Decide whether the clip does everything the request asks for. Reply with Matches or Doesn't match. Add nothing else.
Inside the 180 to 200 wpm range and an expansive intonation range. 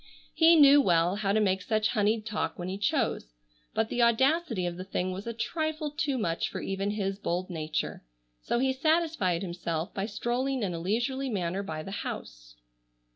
Matches